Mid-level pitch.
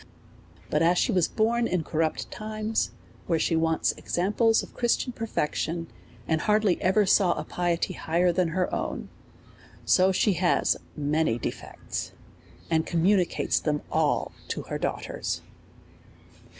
Yes: medium, 180 Hz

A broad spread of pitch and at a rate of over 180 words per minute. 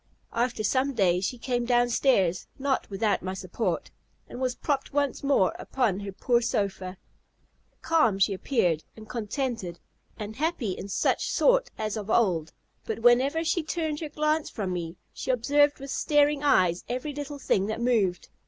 No: wide, 6.2 semitones; average, 165 wpm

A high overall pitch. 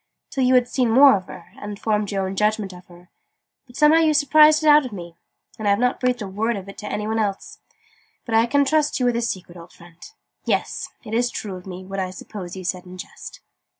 Yes: high, 210 Hz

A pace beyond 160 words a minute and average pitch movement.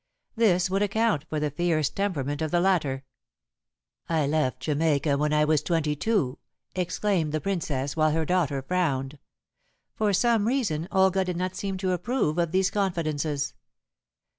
No: average, 155 wpm; average, 4.2 semitones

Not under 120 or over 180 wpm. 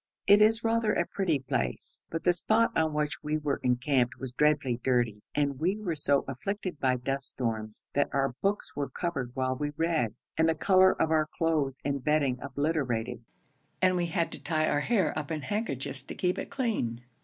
No: average, 195 wpm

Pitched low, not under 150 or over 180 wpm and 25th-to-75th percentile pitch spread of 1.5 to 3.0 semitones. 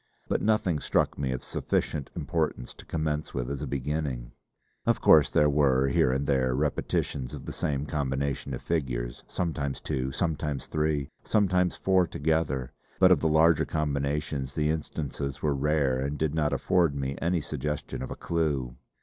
Yes: very low, 75 Hz; average, 165 wpm; average, 2.7 semitones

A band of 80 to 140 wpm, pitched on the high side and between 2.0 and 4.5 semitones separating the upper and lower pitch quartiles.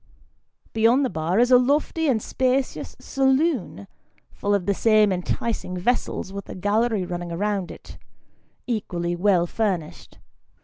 No: slow, 135 wpm; high, 210 Hz; wide, 5.5 semitones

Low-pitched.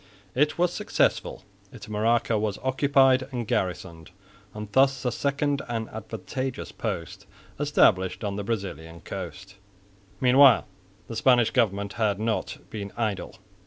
Yes: low, 110 Hz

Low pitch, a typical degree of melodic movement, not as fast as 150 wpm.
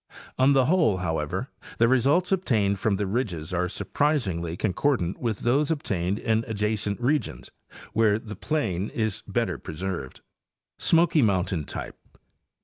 No: low, 110 Hz; wide, 6.3 semitones; average, 140 wpm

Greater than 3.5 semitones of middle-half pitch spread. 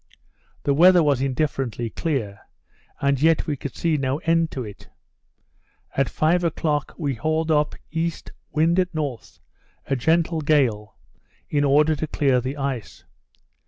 No: average, 3.1 semitones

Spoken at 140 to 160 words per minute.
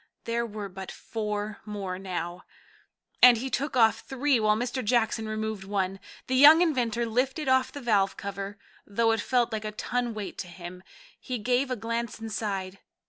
No: average, 175 wpm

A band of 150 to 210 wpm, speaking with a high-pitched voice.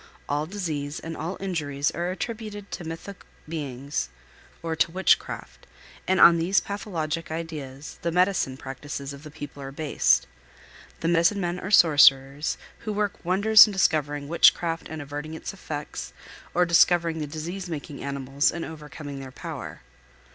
No: average, 155 wpm; medium, 160 Hz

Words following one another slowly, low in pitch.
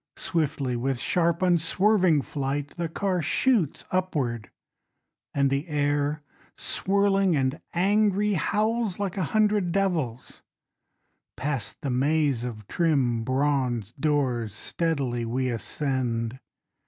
No: slow, 105 wpm; medium, 145 Hz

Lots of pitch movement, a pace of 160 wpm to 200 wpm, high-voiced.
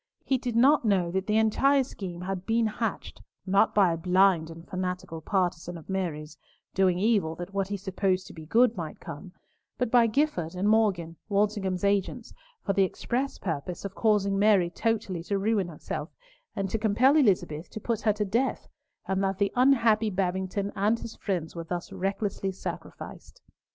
No: average, 3.3 semitones; average, 175 wpm; high, 195 Hz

